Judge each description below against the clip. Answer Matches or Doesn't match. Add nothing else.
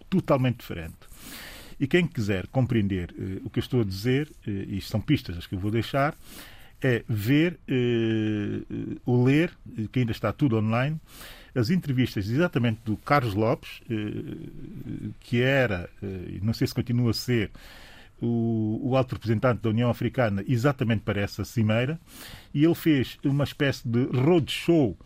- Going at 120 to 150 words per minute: Doesn't match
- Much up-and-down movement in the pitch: Doesn't match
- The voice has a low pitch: Matches